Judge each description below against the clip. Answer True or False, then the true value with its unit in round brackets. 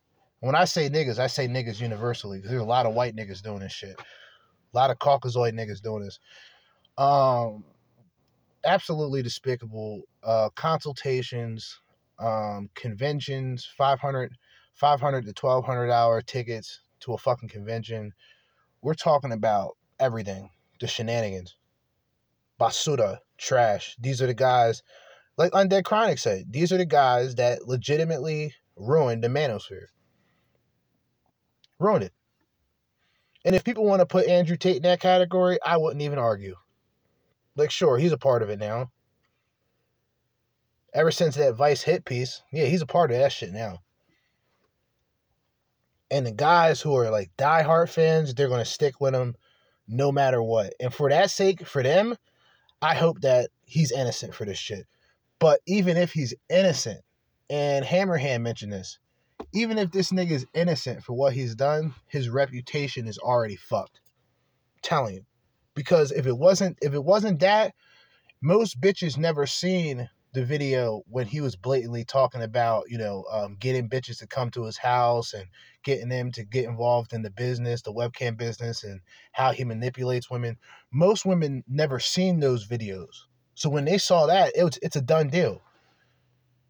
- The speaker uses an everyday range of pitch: True (4.8 semitones)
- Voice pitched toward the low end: True (130 Hz)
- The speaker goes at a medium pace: True (160 wpm)